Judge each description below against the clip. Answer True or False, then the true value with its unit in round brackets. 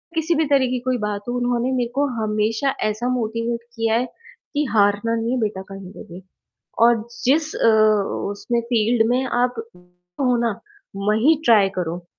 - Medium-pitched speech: False (230 Hz)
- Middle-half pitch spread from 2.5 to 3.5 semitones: True (2.9 semitones)